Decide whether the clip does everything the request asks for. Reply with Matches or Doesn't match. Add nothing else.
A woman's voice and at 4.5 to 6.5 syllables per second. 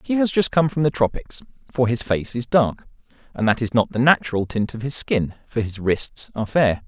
Doesn't match